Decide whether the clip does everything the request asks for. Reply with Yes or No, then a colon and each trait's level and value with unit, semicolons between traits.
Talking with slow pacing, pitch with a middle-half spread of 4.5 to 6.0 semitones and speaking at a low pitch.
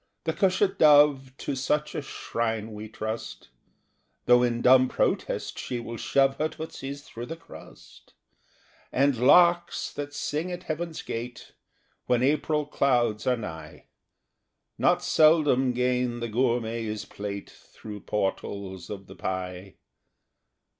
Yes: slow, 125 wpm; average, 5.1 semitones; low, 125 Hz